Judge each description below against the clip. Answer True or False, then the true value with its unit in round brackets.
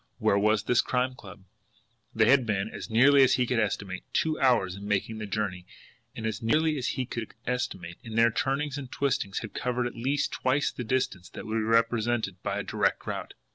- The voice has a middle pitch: False (115 Hz)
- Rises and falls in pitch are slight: False (3.8 semitones)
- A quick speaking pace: True (210 wpm)